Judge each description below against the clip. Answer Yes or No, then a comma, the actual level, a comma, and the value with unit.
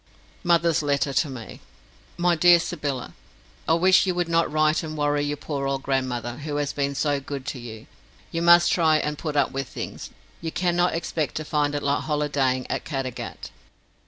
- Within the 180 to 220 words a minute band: Yes, average, 190 wpm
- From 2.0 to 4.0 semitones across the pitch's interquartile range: Yes, average, 3.2 semitones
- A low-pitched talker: No, medium, 145 Hz